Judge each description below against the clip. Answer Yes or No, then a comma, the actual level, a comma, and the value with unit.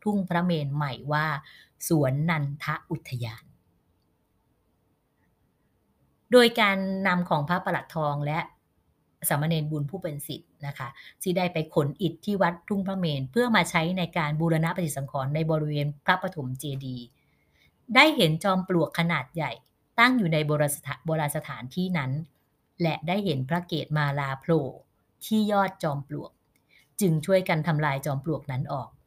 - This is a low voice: No, medium, 155 Hz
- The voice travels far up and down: No, average, 3.8 semitones